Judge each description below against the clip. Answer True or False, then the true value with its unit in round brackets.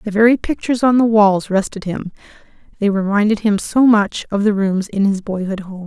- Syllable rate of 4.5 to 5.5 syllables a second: True (5.3 syllables/s)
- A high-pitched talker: True (205 Hz)